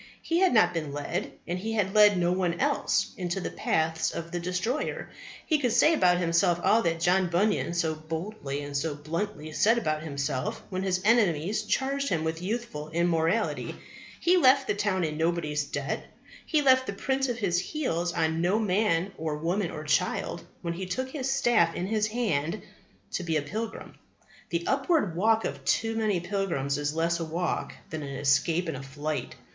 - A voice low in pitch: No, medium, 175 Hz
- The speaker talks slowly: No, average, 190 wpm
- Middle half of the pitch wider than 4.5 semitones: Yes, average, 5.2 semitones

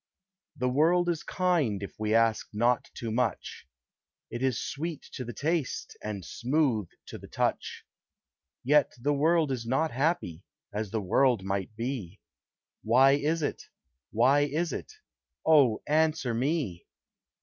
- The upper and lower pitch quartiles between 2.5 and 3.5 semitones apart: No, wide, 5.5 semitones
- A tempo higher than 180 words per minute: No, average, 140 wpm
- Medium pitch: No, low, 130 Hz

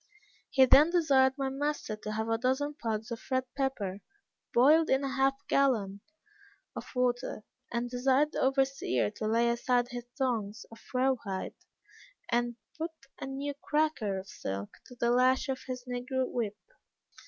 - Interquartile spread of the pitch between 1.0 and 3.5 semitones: Yes, average, 3.0 semitones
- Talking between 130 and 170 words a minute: Yes, average, 160 wpm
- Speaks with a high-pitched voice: Yes, very high, 250 Hz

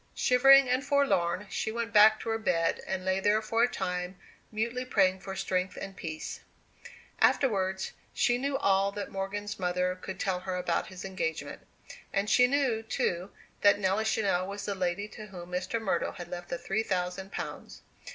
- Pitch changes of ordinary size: Yes, average, 3.3 semitones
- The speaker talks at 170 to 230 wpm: Yes, average, 180 wpm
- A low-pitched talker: No, high, 195 Hz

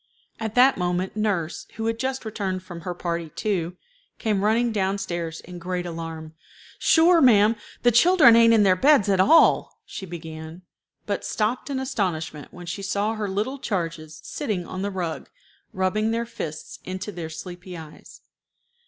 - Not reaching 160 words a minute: No, average, 165 wpm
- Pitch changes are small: No, average, 4.5 semitones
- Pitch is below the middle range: No, high, 190 Hz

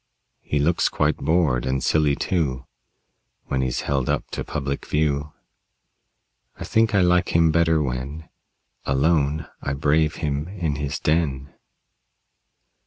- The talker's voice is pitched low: Yes, very low, 75 Hz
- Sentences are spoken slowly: Yes, slow, 130 wpm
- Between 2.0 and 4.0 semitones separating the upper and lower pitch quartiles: Yes, average, 2.9 semitones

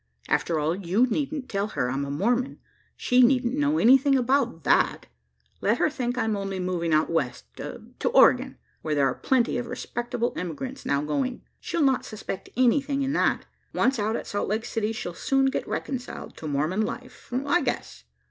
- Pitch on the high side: Yes, high, 235 Hz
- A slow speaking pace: No, average, 180 wpm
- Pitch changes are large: Yes, wide, 6.6 semitones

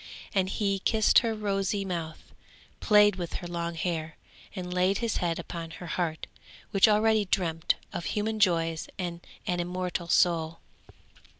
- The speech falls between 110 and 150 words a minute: Yes, average, 145 wpm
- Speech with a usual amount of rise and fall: Yes, average, 3.2 semitones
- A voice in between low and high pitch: Yes, medium, 180 Hz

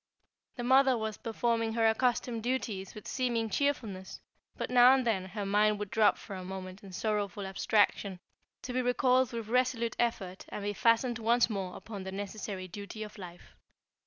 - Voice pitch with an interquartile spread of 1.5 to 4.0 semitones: Yes, average, 3.5 semitones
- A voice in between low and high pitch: No, high, 220 Hz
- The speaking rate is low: No, average, 175 wpm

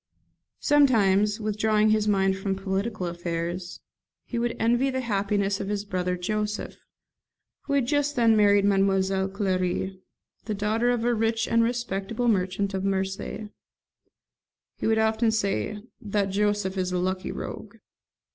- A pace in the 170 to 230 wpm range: No, average, 145 wpm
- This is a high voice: Yes, high, 205 Hz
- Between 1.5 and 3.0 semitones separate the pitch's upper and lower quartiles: Yes, average, 2.7 semitones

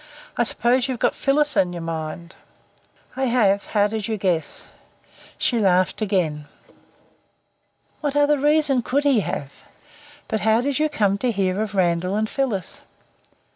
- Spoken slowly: No, average, 150 wpm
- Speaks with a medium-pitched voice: No, high, 220 Hz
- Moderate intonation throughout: No, wide, 6.2 semitones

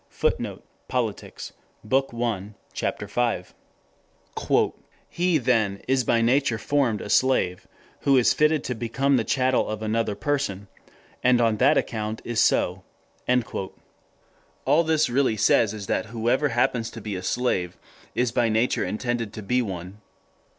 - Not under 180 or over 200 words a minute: No, average, 145 wpm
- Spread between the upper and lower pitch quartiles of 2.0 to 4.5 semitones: Yes, average, 3.3 semitones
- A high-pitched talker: No, low, 120 Hz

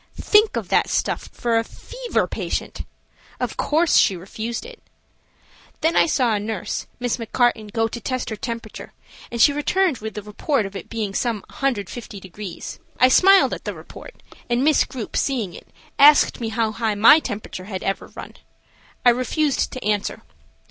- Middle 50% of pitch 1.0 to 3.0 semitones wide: No, average, 4.6 semitones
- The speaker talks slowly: No, average, 175 wpm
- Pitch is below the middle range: No, high, 235 Hz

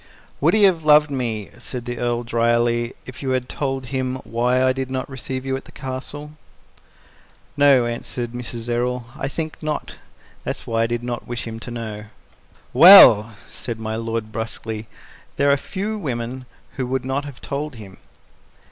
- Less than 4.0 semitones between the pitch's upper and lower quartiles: Yes, narrow, 2.5 semitones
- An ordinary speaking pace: Yes, average, 175 wpm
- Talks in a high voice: No, low, 125 Hz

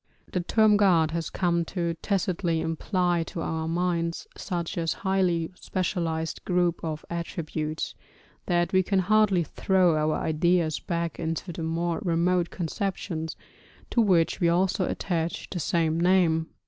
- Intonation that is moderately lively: No, narrow, 1.9 semitones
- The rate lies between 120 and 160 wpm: Yes, average, 140 wpm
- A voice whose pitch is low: No, medium, 170 Hz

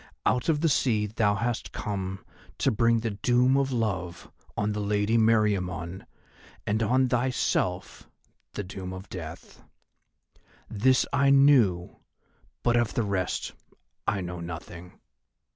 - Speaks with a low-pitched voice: Yes, low, 105 Hz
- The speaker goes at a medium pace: No, slow, 130 wpm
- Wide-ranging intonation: No, average, 4.5 semitones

